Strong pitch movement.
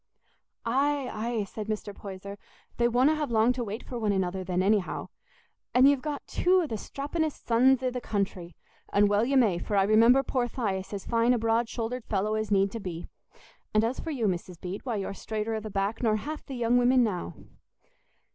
No: average, 3.9 semitones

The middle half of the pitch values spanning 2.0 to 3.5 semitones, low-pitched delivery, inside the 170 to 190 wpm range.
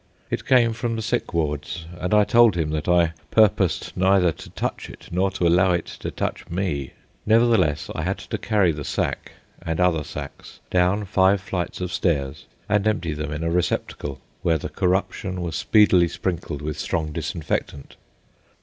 No: average, 3.9 semitones; very low, 90 Hz; average, 175 wpm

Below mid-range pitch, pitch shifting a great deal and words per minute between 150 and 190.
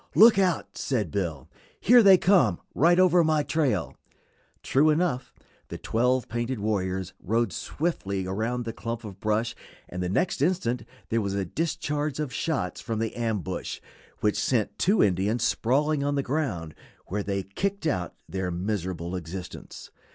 Yes: low, 115 Hz; wide, 7.6 semitones; average, 155 wpm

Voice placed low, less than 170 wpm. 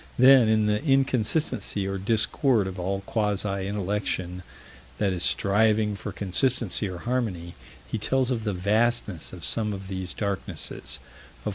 Yes: low, 105 Hz; average, 140 wpm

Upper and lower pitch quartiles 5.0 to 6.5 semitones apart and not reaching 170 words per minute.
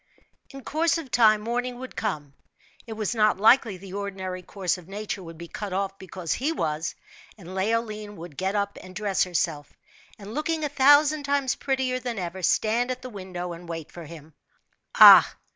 No: average, 5.3 semitones; average, 185 wpm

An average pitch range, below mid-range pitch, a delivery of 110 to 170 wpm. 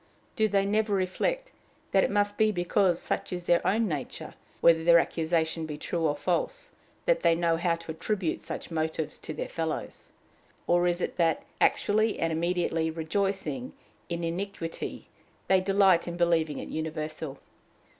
No: average, 3.4 semitones; medium, 175 Hz; average, 160 wpm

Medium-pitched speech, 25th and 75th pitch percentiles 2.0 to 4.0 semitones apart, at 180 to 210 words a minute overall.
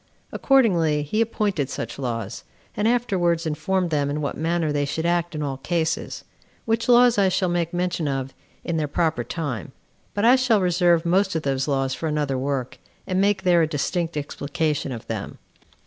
No: medium, 165 Hz; average, 4.5 semitones; average, 185 wpm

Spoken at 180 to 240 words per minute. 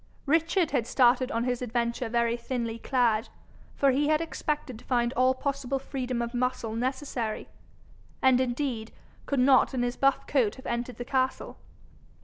No: average, 160 wpm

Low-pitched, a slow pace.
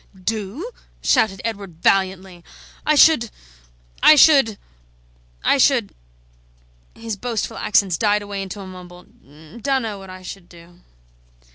No: high, 195 Hz; slow, 125 wpm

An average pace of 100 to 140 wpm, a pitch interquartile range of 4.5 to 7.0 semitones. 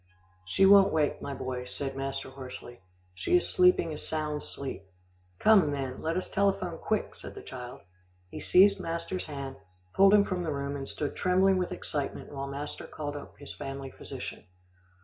No: average, 175 wpm; average, 4.9 semitones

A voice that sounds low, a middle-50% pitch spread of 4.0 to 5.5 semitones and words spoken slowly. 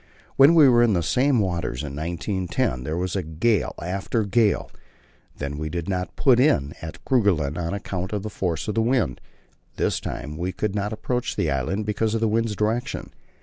No: low, 100 Hz; average, 5.2 semitones; average, 190 wpm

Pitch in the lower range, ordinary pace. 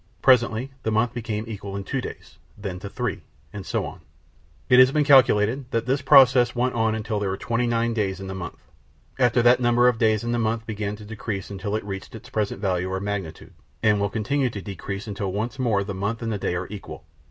No: low, 110 Hz; fast, 230 wpm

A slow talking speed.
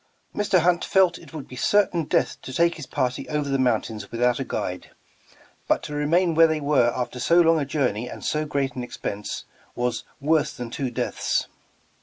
No: average, 200 wpm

